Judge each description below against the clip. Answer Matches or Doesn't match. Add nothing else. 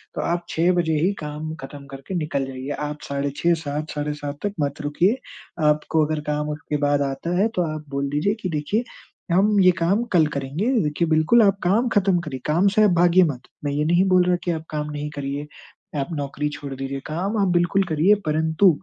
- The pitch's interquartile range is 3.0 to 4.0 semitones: Matches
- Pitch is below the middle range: Doesn't match